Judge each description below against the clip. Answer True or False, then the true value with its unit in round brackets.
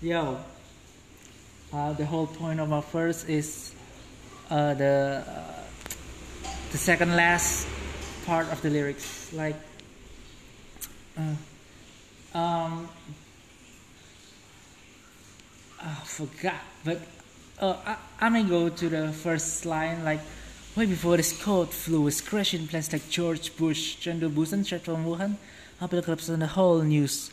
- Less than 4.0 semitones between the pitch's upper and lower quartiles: True (2.7 semitones)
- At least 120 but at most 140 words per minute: True (125 wpm)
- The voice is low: False (160 Hz)